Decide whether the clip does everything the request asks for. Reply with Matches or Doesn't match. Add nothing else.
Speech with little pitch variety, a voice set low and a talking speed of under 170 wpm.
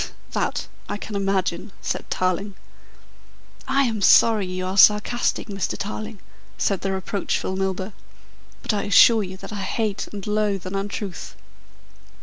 Doesn't match